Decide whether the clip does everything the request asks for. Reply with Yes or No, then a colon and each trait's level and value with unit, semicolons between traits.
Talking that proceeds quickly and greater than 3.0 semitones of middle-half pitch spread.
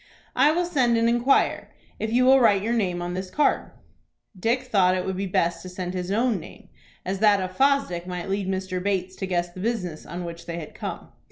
Yes: fast, 225 wpm; average, 4.5 semitones